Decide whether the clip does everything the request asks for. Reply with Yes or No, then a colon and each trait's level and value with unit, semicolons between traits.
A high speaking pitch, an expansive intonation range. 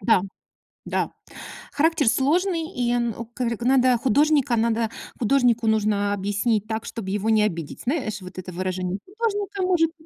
Yes: high, 235 Hz; wide, 6.1 semitones